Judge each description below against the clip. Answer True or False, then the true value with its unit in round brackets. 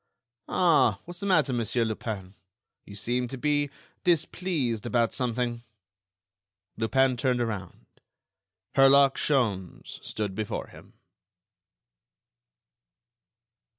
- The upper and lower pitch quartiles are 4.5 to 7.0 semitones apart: False (4.0 semitones)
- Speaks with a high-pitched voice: False (125 Hz)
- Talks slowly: True (90 wpm)